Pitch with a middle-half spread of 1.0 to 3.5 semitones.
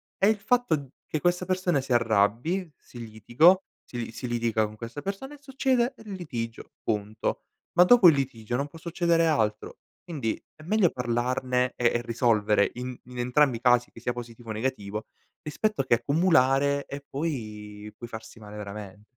No: wide, 6.6 semitones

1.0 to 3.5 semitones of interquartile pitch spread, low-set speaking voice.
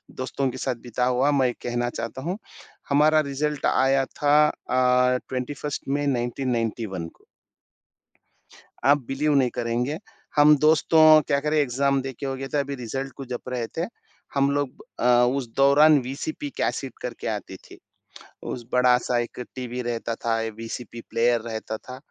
Yes: average, 2.8 semitones; low, 130 Hz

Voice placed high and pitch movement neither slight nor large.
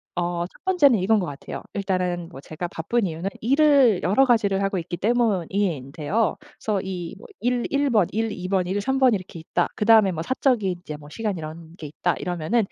Yes: high, 195 Hz; average, 4.9 semitones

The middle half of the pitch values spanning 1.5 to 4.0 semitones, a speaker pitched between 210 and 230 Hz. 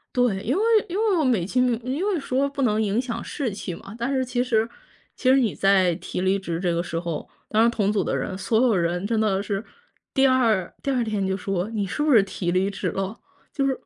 No: average, 4.9 semitones; high, 220 Hz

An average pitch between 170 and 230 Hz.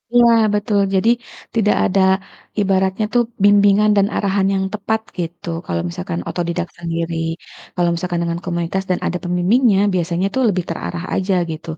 Yes: high, 190 Hz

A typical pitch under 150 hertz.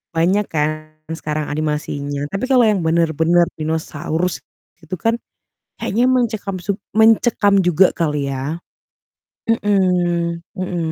No: medium, 170 Hz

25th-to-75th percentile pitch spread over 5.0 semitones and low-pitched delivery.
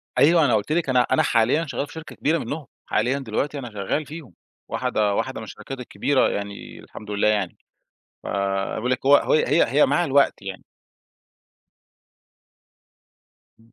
Yes: wide, 5.6 semitones; low, 130 Hz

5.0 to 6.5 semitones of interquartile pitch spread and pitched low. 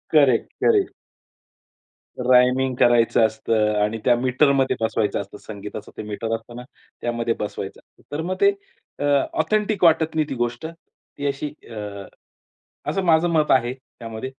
Yes: wide, 5.5 semitones; low, 125 Hz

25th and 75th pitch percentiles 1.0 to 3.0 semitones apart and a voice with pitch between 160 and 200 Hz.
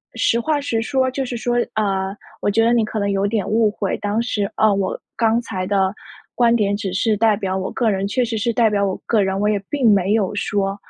No: average, 2.7 semitones; high, 210 Hz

